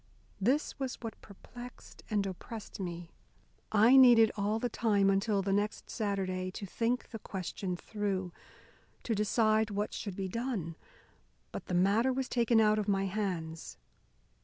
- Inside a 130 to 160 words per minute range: Yes, average, 150 wpm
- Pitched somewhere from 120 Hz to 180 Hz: No, high, 210 Hz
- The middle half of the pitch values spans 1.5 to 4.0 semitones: Yes, average, 2.8 semitones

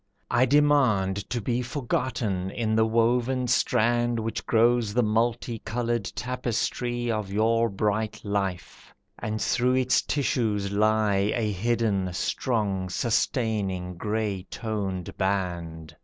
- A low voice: Yes, low, 110 Hz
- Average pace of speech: No, slow, 115 wpm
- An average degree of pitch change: Yes, average, 3.2 semitones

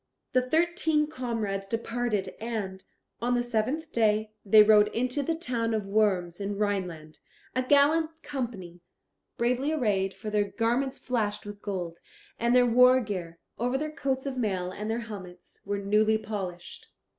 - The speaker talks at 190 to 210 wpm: No, average, 155 wpm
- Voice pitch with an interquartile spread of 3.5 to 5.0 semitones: Yes, average, 4.1 semitones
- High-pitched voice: Yes, high, 220 Hz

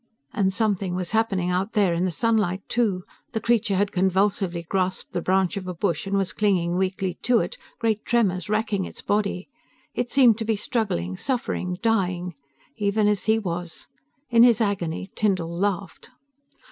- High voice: Yes, high, 195 Hz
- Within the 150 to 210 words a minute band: Yes, average, 170 wpm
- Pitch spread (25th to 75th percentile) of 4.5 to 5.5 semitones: No, average, 3.2 semitones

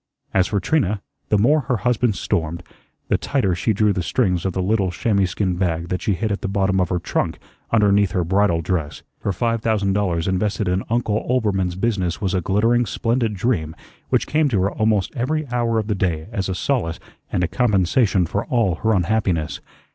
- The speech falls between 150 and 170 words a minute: No, average, 200 wpm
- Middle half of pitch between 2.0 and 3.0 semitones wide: No, average, 3.7 semitones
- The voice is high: No, low, 100 Hz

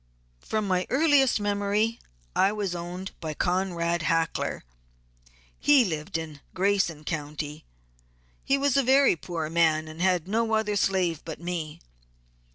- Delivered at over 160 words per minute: No, slow, 135 wpm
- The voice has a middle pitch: Yes, medium, 180 Hz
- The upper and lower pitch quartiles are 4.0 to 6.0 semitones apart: Yes, average, 4.6 semitones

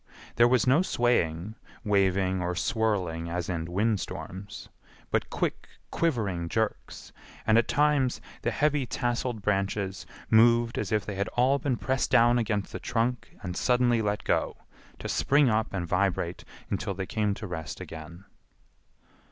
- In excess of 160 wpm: No, average, 150 wpm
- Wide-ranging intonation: No, average, 4.3 semitones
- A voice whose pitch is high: No, low, 105 Hz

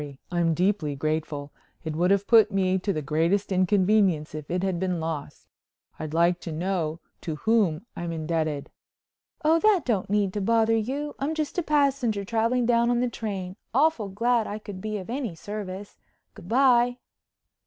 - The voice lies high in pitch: Yes, high, 195 Hz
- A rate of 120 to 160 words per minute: No, average, 175 wpm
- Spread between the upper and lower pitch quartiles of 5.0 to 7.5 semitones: Yes, wide, 5.5 semitones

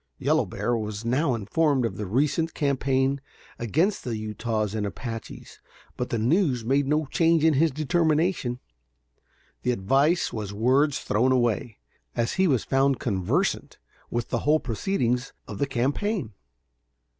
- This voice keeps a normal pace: Yes, average, 145 wpm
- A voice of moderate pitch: No, low, 130 Hz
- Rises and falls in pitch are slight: No, average, 4.7 semitones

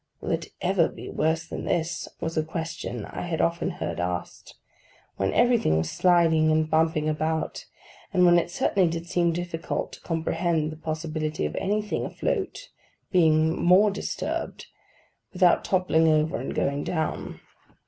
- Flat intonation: Yes, narrow, 2.0 semitones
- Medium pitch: Yes, medium, 160 Hz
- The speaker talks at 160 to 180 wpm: No, average, 150 wpm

